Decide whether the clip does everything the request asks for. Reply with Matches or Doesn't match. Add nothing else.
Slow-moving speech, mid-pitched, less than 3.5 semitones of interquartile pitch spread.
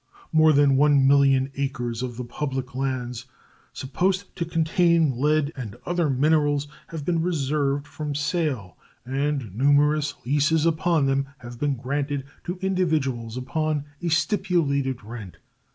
Matches